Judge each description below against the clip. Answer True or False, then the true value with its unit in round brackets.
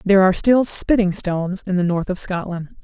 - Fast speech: True (210 wpm)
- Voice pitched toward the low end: False (190 Hz)